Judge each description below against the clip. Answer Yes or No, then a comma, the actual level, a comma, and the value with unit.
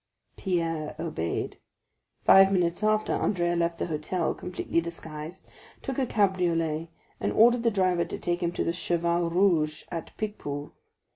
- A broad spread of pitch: No, narrow, 2.5 semitones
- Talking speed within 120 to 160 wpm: Yes, average, 145 wpm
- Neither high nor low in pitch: Yes, medium, 170 Hz